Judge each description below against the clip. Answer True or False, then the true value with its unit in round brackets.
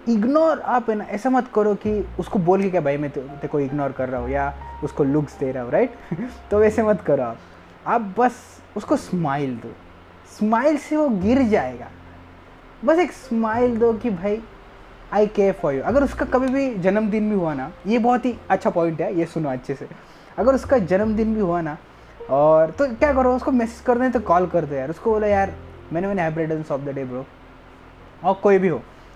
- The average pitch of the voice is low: False (195 Hz)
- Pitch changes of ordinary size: False (8.2 semitones)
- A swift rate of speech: True (210 wpm)